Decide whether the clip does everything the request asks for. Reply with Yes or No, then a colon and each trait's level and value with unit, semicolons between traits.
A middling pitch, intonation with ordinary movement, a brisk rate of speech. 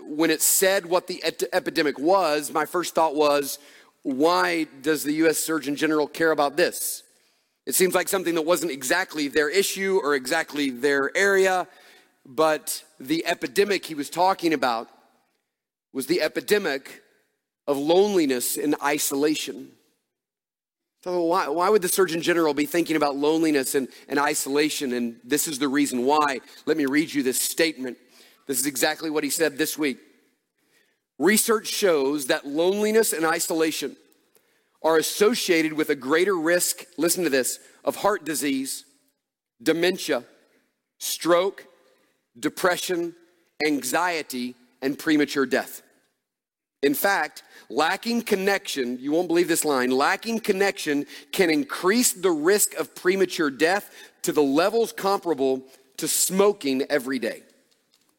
No: medium, 160 Hz; average, 4.1 semitones; slow, 135 wpm